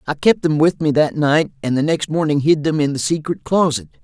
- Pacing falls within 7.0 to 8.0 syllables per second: No, 5.4 syllables/s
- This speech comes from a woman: No, male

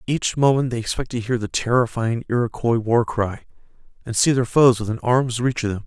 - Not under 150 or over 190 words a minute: No, fast, 205 wpm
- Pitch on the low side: Yes, low, 120 Hz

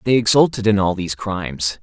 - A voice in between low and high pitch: No, low, 105 Hz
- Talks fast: No, average, 195 wpm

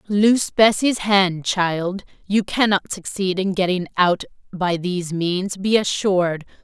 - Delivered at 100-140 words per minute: Yes, slow, 135 wpm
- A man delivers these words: No, female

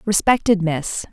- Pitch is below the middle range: No, high, 190 Hz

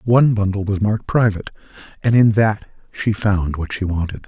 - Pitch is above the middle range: No, low, 105 Hz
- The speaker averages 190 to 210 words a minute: No, average, 180 wpm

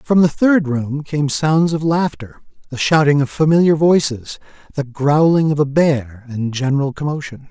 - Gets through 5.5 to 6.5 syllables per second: No, 4.6 syllables/s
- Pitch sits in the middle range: Yes, medium, 145 Hz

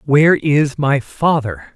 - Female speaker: No, male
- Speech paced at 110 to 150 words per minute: Yes, slow, 135 wpm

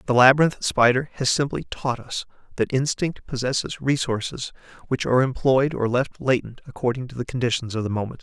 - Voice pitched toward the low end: Yes, low, 125 Hz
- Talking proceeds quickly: No, average, 175 wpm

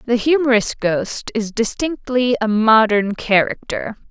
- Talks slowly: Yes, slow, 115 wpm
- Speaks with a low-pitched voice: No, high, 230 Hz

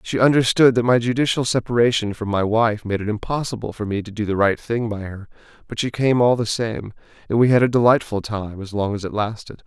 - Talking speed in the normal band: No, fast, 230 wpm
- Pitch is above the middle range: No, low, 115 Hz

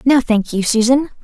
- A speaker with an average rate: Yes, average, 195 wpm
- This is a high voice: Yes, high, 240 Hz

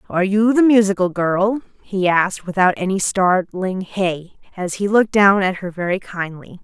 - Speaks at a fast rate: No, average, 170 wpm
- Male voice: No, female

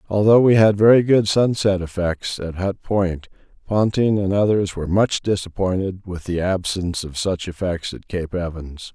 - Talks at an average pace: Yes, average, 170 wpm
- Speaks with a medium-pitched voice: No, very low, 95 Hz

